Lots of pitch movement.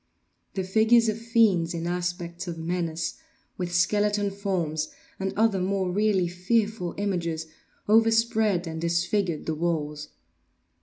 No: average, 3.6 semitones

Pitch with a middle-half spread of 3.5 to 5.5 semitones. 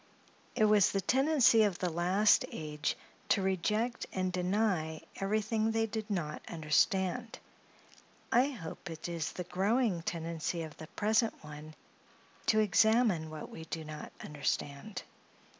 Yes: average, 5.2 semitones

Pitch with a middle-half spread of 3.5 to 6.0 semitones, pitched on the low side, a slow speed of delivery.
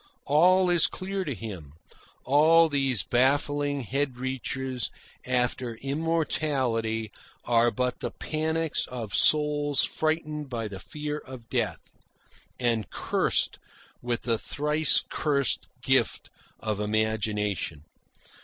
Yes: average, 4.8 semitones; low, 130 Hz; slow, 105 wpm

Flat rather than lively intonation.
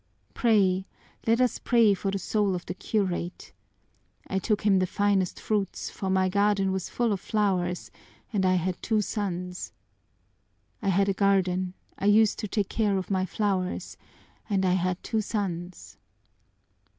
Yes: narrow, 2.1 semitones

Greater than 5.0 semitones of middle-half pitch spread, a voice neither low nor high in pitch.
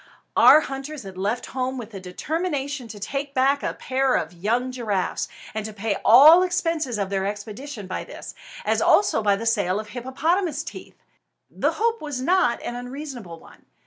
No: wide, 5.6 semitones; very high, 250 Hz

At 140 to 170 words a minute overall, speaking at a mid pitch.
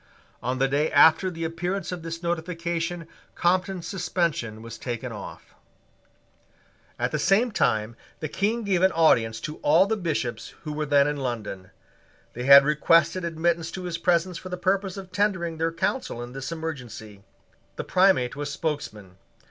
Yes: average, 165 wpm; medium, 165 Hz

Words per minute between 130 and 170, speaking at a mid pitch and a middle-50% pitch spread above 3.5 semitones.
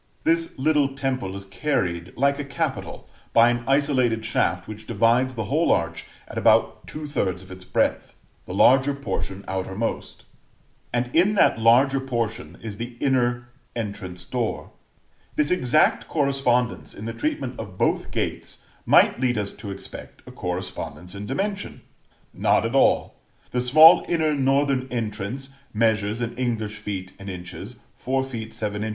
No: average, 150 wpm; low, 120 Hz; average, 4.9 semitones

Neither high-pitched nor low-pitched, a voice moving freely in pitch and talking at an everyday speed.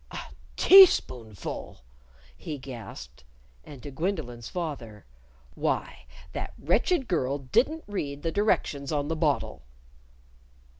No: medium, 145 Hz; wide, 5.9 semitones; slow, 105 wpm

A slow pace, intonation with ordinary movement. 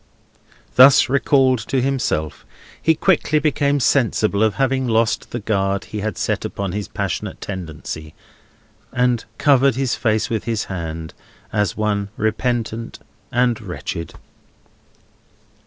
Yes: slow, 125 wpm; average, 4.5 semitones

